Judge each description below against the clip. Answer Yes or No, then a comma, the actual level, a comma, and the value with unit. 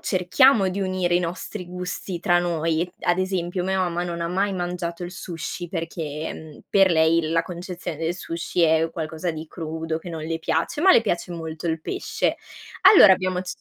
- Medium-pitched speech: Yes, medium, 175 Hz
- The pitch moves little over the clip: Yes, narrow, 2.0 semitones